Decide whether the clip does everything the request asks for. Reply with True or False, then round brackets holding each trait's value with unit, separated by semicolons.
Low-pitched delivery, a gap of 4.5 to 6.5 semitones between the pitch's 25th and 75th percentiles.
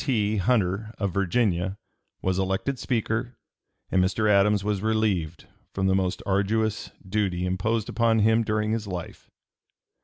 False (105 Hz; 2.7 semitones)